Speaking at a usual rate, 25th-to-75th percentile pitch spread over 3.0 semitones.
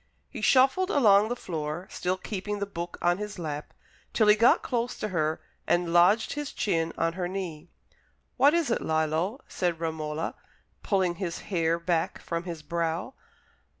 Yes: average, 165 wpm; average, 4.2 semitones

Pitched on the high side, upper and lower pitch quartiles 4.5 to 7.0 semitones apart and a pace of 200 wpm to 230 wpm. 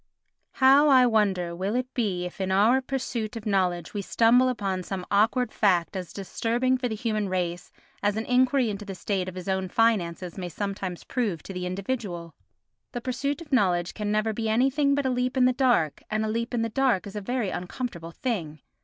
Yes: high, 215 Hz; average, 5.0 semitones; fast, 205 wpm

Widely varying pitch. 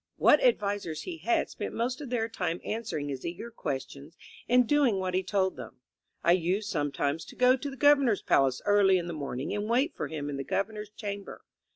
Yes: wide, 6.5 semitones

